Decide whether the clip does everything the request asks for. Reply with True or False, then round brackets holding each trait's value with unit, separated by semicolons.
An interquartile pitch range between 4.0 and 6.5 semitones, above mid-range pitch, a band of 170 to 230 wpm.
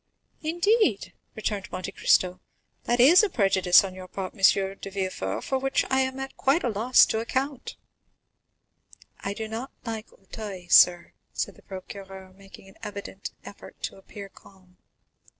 False (4.8 semitones; 200 Hz; 155 wpm)